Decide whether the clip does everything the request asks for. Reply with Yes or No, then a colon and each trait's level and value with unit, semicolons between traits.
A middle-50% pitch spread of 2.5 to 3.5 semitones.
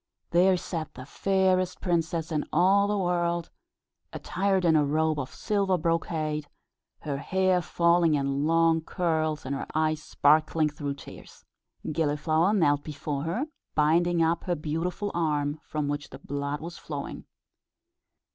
Yes: average, 2.8 semitones